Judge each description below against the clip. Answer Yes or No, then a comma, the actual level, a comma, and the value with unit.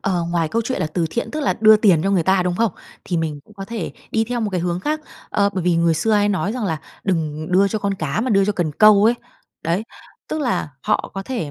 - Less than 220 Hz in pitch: Yes, high, 195 Hz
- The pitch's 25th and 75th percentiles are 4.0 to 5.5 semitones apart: Yes, average, 4.4 semitones